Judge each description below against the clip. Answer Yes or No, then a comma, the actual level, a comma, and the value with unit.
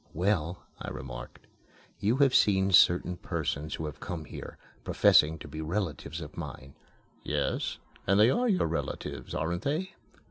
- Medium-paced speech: Yes, average, 150 wpm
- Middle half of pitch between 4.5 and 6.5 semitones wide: Yes, average, 5.2 semitones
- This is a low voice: Yes, very low, 85 Hz